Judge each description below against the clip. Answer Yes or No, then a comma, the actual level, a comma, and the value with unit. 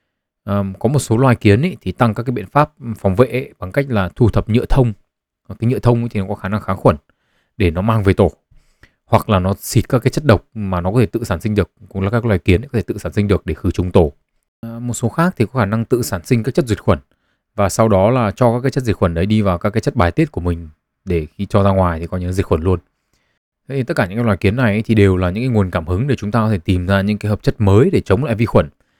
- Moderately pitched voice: No, low, 105 Hz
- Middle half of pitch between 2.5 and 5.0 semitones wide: Yes, average, 4.0 semitones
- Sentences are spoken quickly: Yes, fast, 310 wpm